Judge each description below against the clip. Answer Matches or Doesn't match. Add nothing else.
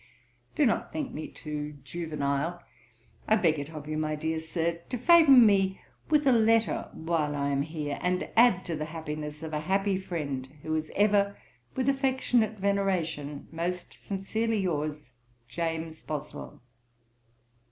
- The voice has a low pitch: Doesn't match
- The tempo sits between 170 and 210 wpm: Doesn't match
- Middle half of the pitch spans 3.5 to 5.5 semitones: Matches